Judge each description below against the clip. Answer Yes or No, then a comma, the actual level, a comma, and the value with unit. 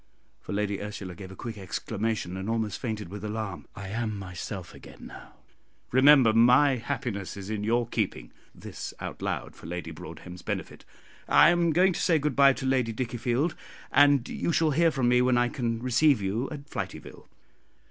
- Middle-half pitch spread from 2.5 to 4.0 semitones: No, average, 4.9 semitones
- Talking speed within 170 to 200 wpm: Yes, average, 180 wpm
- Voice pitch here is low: Yes, low, 115 Hz